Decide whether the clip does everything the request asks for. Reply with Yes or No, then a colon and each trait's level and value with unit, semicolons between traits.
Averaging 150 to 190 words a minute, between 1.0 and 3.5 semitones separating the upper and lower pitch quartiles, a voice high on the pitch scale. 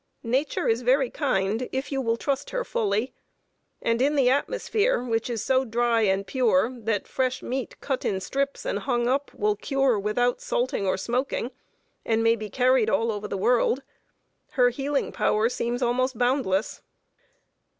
Yes: average, 165 wpm; average, 3.0 semitones; high, 245 Hz